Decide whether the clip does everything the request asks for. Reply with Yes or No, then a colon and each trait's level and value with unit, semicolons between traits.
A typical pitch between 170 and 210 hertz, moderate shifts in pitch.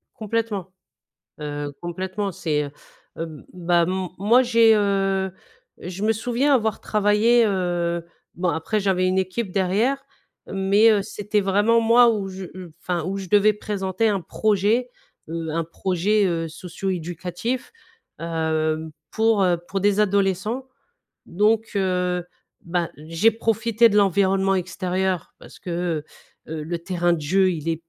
Yes: high, 190 Hz; average, 3.4 semitones